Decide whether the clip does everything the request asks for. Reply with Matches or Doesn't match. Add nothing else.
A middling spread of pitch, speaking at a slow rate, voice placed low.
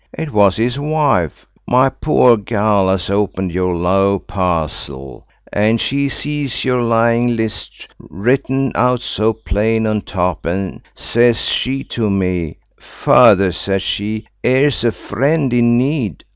Matches